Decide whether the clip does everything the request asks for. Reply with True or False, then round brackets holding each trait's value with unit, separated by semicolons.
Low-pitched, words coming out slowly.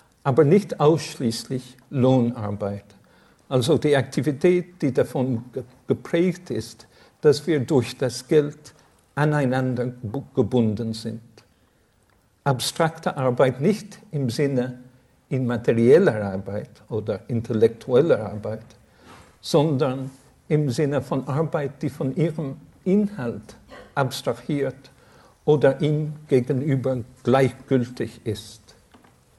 True (130 Hz; 90 wpm)